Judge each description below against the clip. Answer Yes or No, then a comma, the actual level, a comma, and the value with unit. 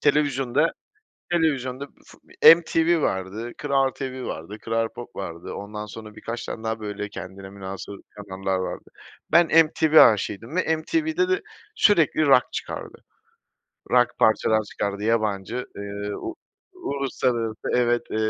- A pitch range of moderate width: No, wide, 6.0 semitones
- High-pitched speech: No, low, 120 Hz